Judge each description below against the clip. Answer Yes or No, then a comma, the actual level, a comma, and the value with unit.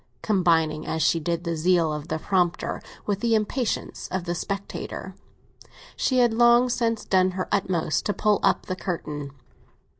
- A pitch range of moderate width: Yes, average, 4.3 semitones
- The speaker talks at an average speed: Yes, average, 160 wpm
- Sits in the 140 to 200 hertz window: Yes, medium, 185 Hz